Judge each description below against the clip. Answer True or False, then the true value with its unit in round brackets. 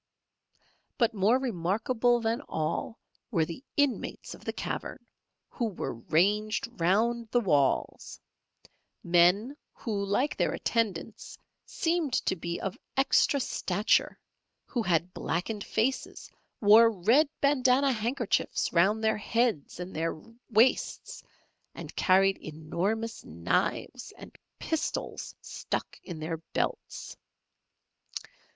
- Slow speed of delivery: True (110 wpm)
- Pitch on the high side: True (215 Hz)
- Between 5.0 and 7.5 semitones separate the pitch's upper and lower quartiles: True (5.3 semitones)